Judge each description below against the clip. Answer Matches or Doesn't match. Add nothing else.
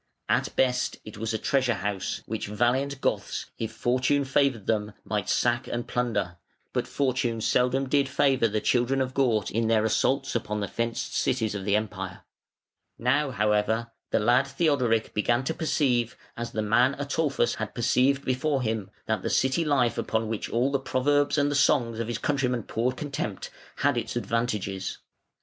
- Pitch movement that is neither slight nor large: Matches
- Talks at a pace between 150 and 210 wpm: Matches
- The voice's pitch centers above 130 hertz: Doesn't match